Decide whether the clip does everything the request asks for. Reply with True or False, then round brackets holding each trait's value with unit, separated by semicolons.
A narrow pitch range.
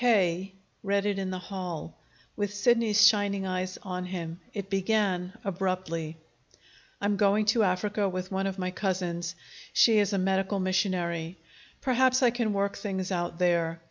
True (2.1 semitones)